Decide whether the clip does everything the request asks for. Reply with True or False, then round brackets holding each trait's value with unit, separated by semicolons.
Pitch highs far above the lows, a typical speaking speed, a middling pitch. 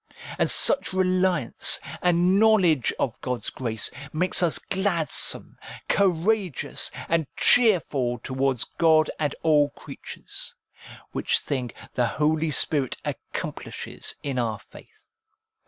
False (5.7 semitones; 110 wpm; 155 Hz)